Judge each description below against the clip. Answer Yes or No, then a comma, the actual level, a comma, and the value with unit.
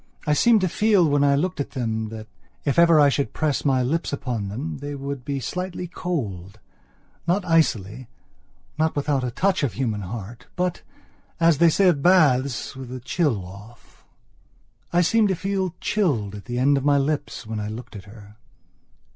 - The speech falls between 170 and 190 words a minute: Yes, average, 185 wpm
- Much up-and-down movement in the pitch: Yes, wide, 6.4 semitones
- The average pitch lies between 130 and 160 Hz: Yes, medium, 140 Hz